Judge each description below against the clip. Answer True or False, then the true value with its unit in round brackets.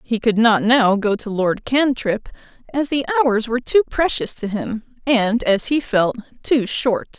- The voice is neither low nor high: False (235 Hz)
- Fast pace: False (185 wpm)